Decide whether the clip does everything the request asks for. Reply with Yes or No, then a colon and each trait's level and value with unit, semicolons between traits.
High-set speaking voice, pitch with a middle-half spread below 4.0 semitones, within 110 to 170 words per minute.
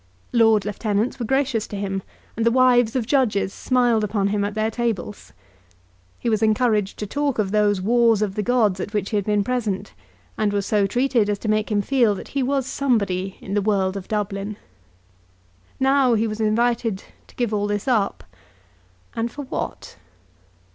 No: high, 215 Hz; average, 3.0 semitones; average, 185 wpm